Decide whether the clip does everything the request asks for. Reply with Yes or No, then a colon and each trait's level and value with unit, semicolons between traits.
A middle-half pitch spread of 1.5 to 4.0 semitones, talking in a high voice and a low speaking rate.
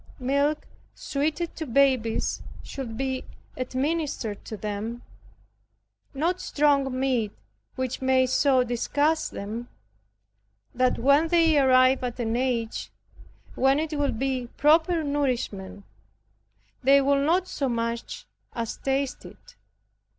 Yes: average, 3.1 semitones; very high, 265 Hz; slow, 115 wpm